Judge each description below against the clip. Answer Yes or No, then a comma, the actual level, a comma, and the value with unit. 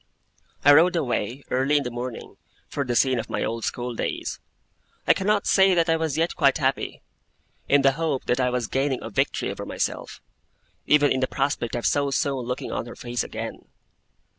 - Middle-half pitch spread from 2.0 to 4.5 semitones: Yes, average, 3.2 semitones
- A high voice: No, low, 135 Hz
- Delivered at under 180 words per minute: No, average, 195 wpm